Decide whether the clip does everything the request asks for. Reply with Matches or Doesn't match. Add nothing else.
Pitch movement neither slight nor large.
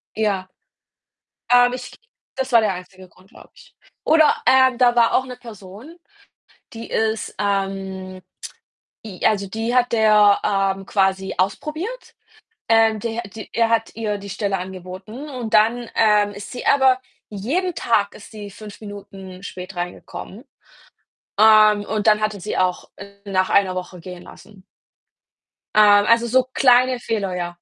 Matches